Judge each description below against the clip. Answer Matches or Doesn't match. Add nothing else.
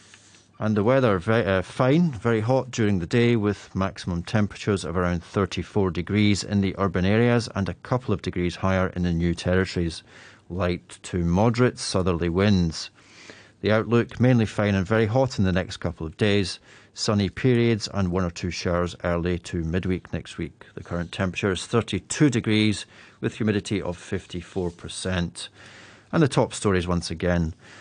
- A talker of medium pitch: Doesn't match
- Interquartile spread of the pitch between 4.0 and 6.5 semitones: Doesn't match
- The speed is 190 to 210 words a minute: Doesn't match